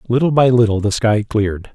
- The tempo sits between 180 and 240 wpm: Yes, fast, 205 wpm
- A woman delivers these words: No, male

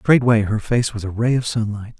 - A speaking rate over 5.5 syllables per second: No, 5.2 syllables/s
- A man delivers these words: Yes, male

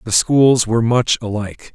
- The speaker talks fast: No, average, 170 wpm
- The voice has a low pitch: Yes, low, 115 Hz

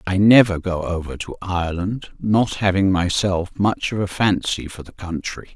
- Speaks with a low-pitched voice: Yes, very low, 95 Hz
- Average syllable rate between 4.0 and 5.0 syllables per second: Yes, 4.6 syllables/s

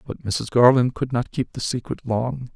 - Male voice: Yes, male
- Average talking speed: No, fast, 210 wpm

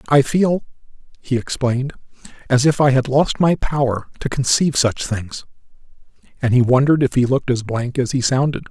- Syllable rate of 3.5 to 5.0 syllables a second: No, 5.5 syllables/s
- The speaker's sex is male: Yes, male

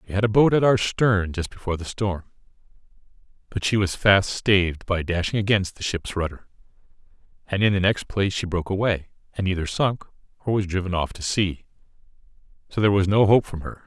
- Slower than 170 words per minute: No, average, 200 wpm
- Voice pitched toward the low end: Yes, very low, 95 Hz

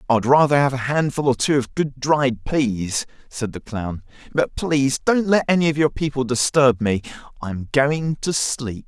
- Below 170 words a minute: No, average, 195 wpm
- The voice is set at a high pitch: No, low, 135 Hz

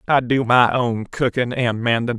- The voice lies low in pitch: Yes, low, 120 Hz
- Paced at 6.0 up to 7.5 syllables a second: No, 4.5 syllables/s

